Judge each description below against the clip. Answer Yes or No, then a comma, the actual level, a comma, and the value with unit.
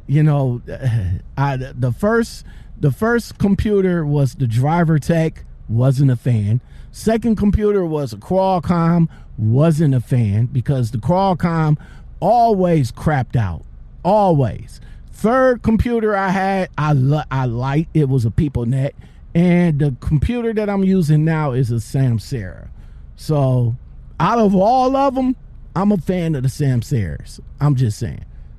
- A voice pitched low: No, medium, 150 Hz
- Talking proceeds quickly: No, average, 145 wpm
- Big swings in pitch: Yes, wide, 6.8 semitones